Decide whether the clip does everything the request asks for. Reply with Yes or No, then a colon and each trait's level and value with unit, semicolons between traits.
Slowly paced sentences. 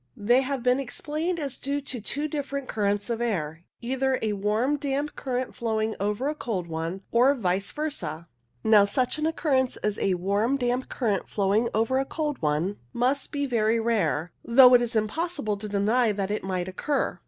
No: average, 185 wpm